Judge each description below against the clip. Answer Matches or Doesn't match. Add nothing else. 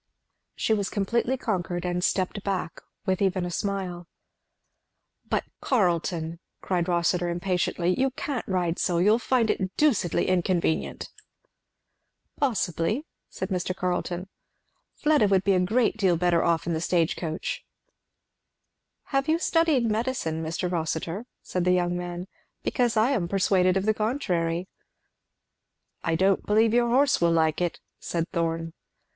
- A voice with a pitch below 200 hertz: Matches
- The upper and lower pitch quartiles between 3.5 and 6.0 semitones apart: Matches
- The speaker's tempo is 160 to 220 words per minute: Doesn't match